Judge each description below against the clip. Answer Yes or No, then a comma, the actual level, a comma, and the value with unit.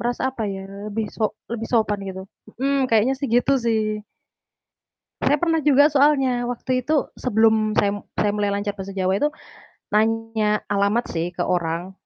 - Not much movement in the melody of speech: No, average, 3.8 semitones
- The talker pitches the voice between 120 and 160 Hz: No, high, 220 Hz